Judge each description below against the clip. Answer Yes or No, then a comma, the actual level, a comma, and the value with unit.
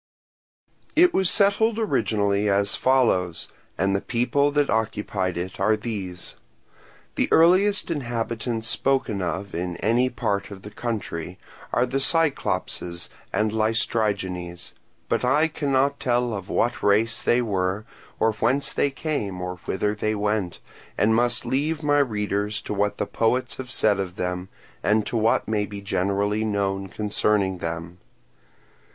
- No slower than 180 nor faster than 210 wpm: No, average, 145 wpm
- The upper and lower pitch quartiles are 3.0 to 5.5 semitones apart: Yes, average, 4.3 semitones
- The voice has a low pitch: Yes, low, 110 Hz